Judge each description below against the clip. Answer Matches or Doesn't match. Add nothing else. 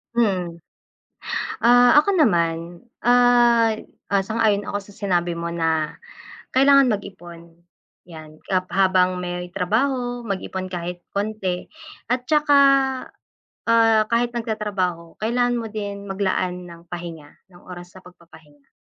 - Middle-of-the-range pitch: Doesn't match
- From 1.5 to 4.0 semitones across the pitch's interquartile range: Doesn't match